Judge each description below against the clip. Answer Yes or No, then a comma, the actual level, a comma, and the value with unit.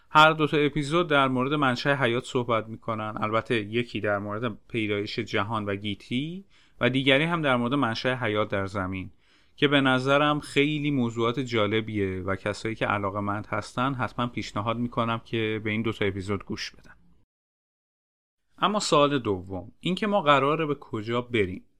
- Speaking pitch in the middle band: No, low, 120 Hz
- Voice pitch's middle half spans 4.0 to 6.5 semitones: Yes, average, 4.8 semitones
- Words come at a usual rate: No, fast, 160 wpm